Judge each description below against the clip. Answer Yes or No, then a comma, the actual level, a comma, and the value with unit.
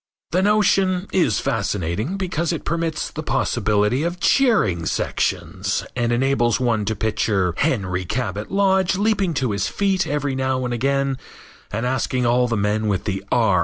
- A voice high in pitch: No, low, 130 Hz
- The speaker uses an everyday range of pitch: No, wide, 8.1 semitones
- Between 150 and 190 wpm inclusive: Yes, average, 160 wpm